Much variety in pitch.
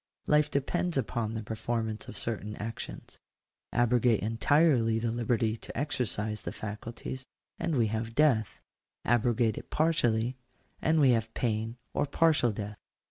No: average, 3.3 semitones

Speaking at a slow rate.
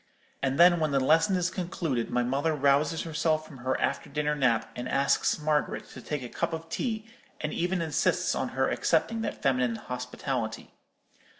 No: average, 180 wpm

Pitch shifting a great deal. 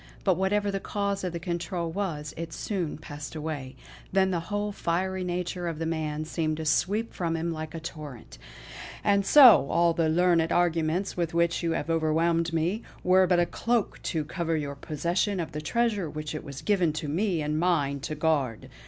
No: average, 3.0 semitones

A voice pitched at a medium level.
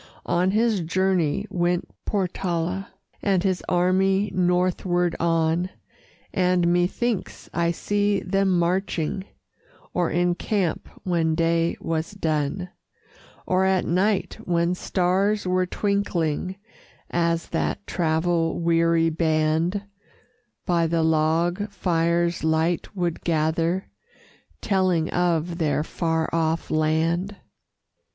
Yes: medium, 175 Hz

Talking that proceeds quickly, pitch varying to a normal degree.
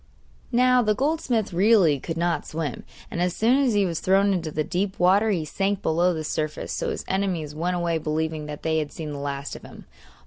Yes: fast, 215 wpm; average, 4.5 semitones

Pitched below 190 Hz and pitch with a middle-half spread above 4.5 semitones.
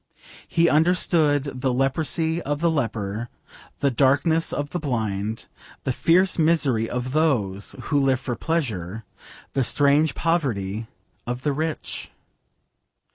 Yes: medium, 140 Hz; average, 5.2 semitones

